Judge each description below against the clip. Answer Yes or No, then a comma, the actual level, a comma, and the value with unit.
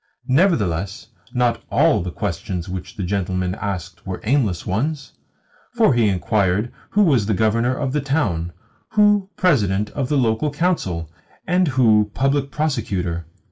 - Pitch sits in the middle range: No, low, 110 Hz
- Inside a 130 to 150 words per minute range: Yes, average, 140 wpm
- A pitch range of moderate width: No, wide, 7.1 semitones